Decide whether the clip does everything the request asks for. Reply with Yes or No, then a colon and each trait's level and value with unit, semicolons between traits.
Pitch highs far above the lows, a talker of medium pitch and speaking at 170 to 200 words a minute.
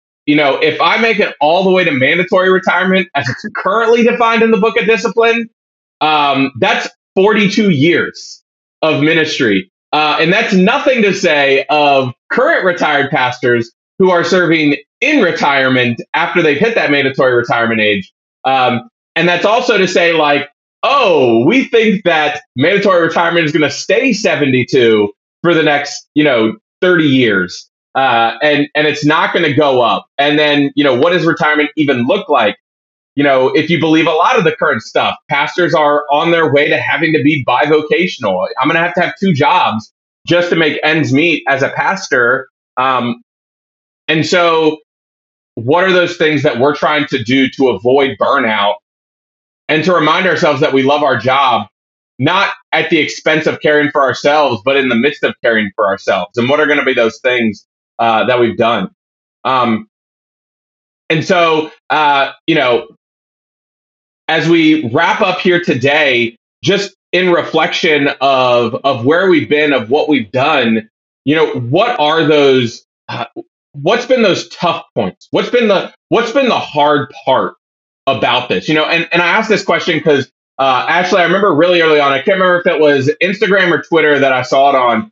No: average, 4.8 semitones; medium, 150 Hz; average, 180 wpm